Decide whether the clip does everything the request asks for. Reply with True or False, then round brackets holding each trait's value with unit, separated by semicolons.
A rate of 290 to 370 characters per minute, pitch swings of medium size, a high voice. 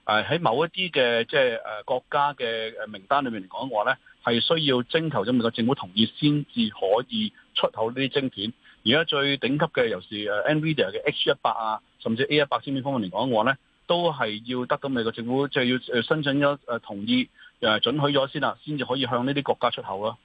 False (340 characters per minute; 4.6 semitones; 140 Hz)